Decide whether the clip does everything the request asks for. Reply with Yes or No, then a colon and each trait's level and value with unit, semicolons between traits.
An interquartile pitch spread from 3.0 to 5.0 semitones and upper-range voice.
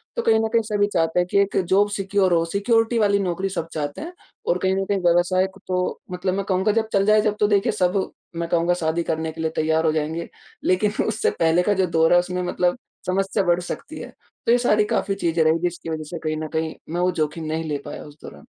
No: average, 3.6 semitones; medium, 180 Hz